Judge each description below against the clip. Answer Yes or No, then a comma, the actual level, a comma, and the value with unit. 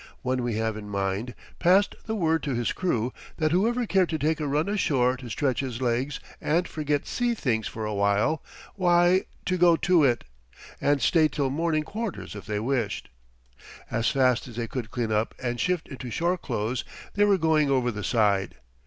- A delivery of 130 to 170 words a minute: No, average, 195 wpm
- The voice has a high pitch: No, low, 135 Hz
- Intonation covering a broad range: Yes, wide, 6.3 semitones